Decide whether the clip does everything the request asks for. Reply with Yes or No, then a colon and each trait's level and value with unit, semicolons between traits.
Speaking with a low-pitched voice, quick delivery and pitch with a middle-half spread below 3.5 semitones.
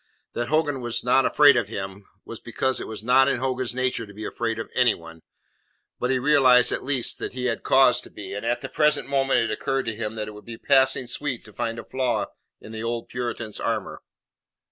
Yes: low, 125 Hz; fast, 225 wpm; average, 2.9 semitones